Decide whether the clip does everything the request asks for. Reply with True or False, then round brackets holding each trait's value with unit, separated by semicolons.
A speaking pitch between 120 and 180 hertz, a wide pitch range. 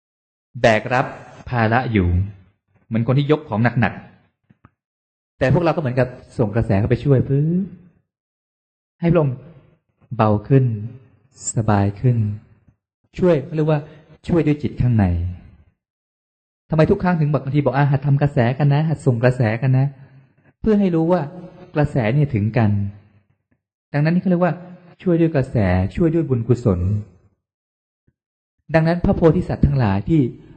True (130 Hz; 6.6 semitones)